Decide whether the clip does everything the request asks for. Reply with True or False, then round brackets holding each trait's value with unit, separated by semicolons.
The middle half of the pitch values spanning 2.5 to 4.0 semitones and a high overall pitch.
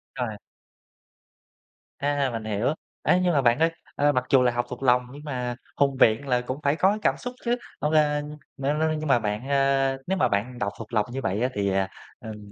False (3.7 semitones; 135 Hz)